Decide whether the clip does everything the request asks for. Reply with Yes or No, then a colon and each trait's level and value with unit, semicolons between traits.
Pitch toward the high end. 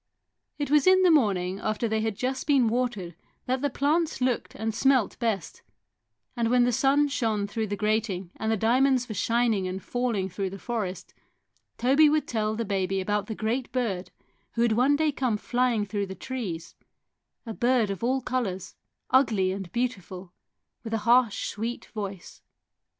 Yes: high, 225 Hz